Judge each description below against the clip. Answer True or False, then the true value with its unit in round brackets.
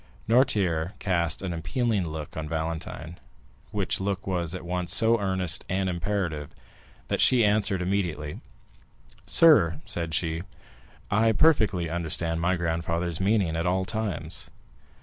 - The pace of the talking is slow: True (130 wpm)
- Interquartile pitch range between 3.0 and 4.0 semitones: True (3.5 semitones)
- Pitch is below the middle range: True (90 Hz)